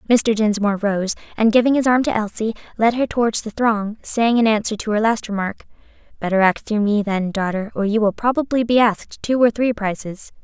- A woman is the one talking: Yes, female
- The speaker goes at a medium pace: No, fast, 215 wpm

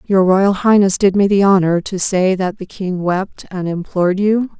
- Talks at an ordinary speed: No, fast, 210 wpm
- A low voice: No, high, 190 Hz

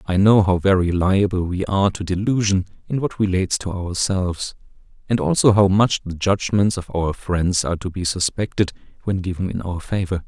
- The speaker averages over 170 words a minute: Yes, average, 185 wpm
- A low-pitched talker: Yes, very low, 95 Hz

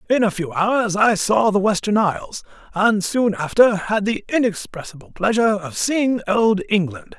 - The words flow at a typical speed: Yes, average, 165 wpm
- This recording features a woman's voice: No, male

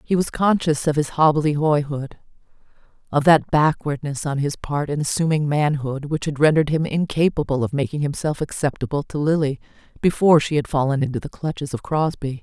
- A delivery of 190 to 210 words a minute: No, average, 165 wpm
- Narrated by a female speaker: Yes, female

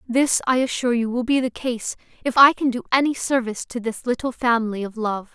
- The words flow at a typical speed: No, fast, 225 wpm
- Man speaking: No, female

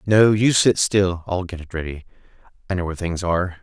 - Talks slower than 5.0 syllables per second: No, 5.8 syllables/s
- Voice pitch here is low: Yes, very low, 95 Hz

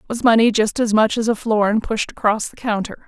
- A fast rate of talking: Yes, fast, 255 wpm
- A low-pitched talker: No, high, 220 Hz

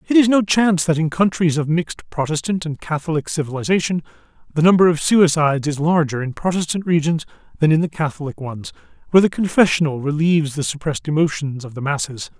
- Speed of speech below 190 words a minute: Yes, average, 180 wpm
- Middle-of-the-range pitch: Yes, medium, 160 Hz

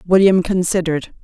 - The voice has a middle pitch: Yes, medium, 180 Hz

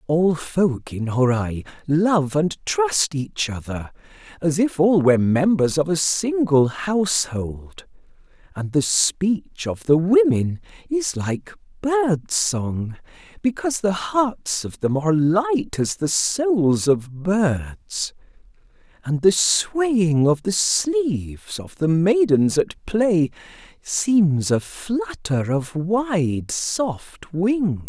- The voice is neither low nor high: Yes, medium, 175 Hz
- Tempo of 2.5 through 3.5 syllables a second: Yes, 3.1 syllables/s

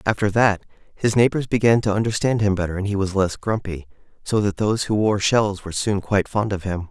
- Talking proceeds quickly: Yes, fast, 225 wpm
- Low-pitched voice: Yes, low, 100 Hz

